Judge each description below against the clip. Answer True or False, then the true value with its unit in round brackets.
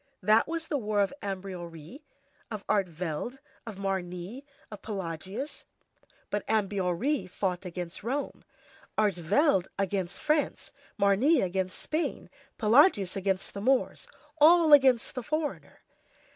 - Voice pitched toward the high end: True (200 Hz)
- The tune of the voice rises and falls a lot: True (6.3 semitones)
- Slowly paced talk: True (115 wpm)